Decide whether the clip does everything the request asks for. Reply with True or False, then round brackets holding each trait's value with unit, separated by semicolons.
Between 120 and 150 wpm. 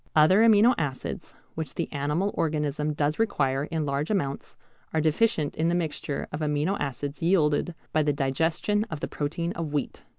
False (170 wpm)